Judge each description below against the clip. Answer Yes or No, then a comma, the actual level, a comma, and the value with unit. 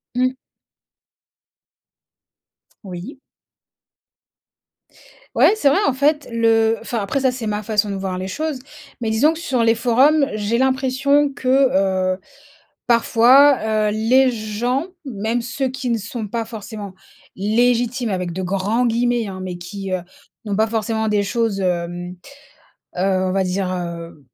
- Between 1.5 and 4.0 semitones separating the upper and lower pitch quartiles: No, average, 4.6 semitones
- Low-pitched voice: No, high, 225 Hz